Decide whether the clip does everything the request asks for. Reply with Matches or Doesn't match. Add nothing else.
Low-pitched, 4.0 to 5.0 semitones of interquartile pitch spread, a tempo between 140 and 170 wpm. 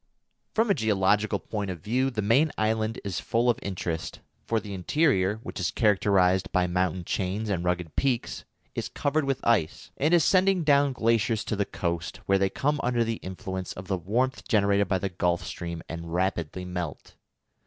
Doesn't match